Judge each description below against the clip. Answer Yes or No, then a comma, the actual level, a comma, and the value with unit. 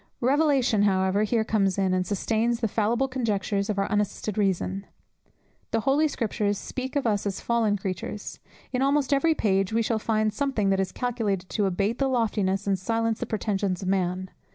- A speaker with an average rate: Yes, average, 180 wpm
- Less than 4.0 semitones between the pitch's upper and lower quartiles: Yes, average, 3.3 semitones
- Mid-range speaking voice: No, high, 210 Hz